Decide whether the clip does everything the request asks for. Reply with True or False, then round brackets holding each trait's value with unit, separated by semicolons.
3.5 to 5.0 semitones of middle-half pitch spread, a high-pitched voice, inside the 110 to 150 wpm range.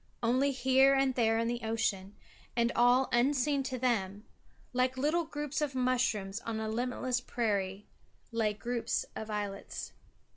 False (3.0 semitones; 240 Hz; 145 wpm)